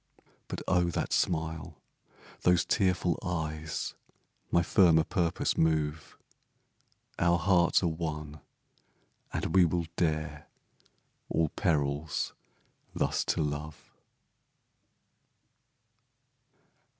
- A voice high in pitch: No, very low, 80 Hz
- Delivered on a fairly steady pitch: Yes, narrow, 2.1 semitones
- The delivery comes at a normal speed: No, slow, 85 wpm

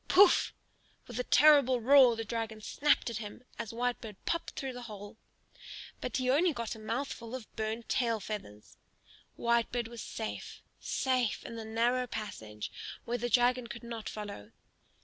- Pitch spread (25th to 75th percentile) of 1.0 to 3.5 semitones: Yes, narrow, 2.5 semitones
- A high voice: Yes, high, 235 Hz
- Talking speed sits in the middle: Yes, average, 160 wpm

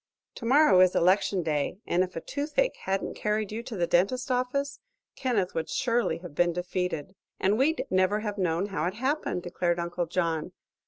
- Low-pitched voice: No, high, 190 Hz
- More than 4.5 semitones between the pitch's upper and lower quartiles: Yes, average, 5.3 semitones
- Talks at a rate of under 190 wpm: Yes, average, 175 wpm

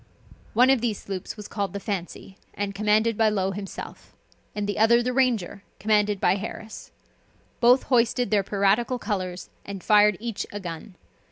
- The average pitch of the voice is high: Yes, high, 210 Hz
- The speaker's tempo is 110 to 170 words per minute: Yes, average, 165 wpm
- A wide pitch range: No, average, 2.7 semitones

